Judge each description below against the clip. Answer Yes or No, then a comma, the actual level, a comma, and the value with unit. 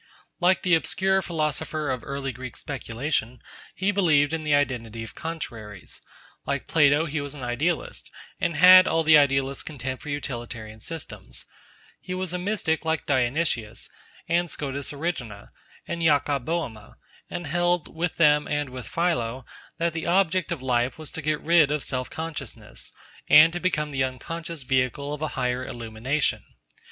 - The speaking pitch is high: No, medium, 150 Hz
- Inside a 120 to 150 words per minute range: No, average, 160 wpm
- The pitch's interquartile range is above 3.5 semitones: Yes, average, 4.3 semitones